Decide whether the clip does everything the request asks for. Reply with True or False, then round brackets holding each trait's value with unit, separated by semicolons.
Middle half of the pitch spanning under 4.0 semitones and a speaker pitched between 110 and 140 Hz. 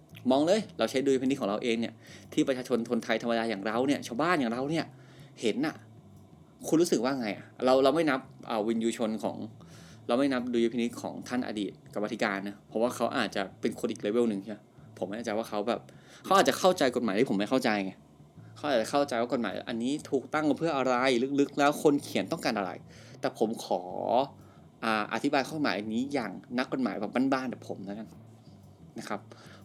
True (3.3 semitones; 120 Hz)